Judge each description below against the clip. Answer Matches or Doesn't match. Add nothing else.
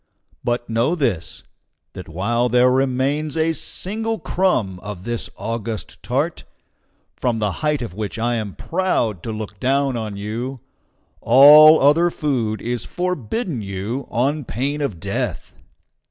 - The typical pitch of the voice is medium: Doesn't match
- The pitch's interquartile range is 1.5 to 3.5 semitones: Doesn't match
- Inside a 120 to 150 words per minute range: Matches